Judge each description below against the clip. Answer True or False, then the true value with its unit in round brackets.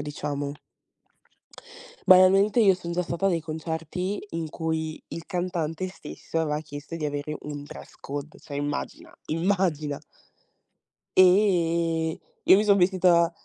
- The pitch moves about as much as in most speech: True (3.3 semitones)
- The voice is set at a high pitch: False (165 Hz)